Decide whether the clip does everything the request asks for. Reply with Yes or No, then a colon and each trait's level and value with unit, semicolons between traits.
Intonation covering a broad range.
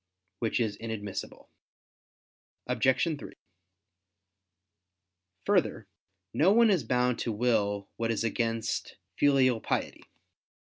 No: average, 2.8 semitones